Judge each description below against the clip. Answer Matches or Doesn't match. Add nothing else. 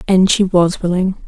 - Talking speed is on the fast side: Doesn't match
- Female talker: Matches